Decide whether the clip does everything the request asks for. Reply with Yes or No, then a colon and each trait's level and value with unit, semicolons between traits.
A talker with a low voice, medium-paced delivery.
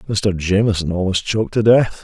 Yes: low, 100 Hz; average, 175 wpm